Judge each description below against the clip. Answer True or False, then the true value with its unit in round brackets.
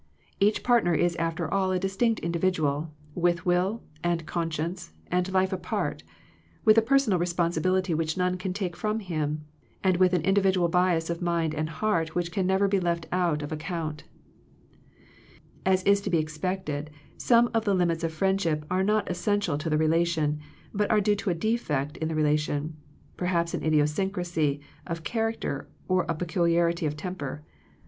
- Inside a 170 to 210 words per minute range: True (180 wpm)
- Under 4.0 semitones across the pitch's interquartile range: True (3.1 semitones)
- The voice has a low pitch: False (175 Hz)